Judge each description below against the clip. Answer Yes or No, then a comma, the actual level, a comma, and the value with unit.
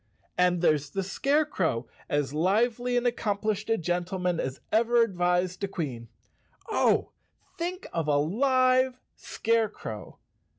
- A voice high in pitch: Yes, high, 195 Hz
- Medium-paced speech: No, slow, 125 wpm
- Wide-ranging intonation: Yes, wide, 6.3 semitones